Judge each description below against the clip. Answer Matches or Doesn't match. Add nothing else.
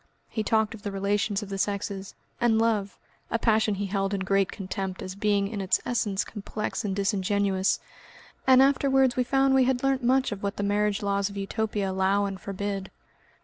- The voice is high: Matches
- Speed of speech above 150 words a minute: Matches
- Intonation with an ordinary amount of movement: Doesn't match